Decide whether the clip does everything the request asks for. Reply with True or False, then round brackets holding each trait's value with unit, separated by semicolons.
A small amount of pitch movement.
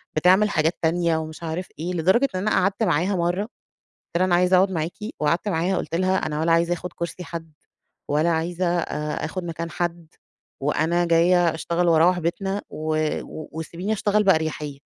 True (2.2 semitones)